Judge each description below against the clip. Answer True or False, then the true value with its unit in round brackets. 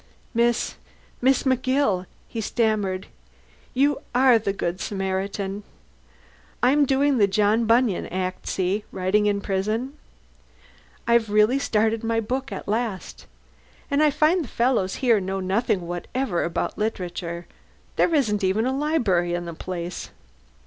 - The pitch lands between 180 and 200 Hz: False (215 Hz)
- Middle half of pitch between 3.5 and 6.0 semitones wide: True (5.1 semitones)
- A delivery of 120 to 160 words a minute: True (135 wpm)